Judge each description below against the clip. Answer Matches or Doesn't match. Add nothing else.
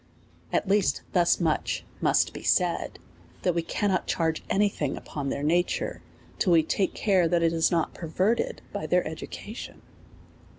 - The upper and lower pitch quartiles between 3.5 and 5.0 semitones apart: Doesn't match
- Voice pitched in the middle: Matches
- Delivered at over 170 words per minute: Doesn't match